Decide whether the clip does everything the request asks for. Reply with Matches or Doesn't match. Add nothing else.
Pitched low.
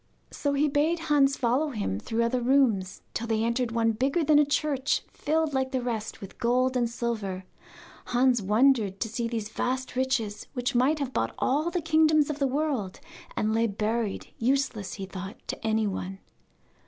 Doesn't match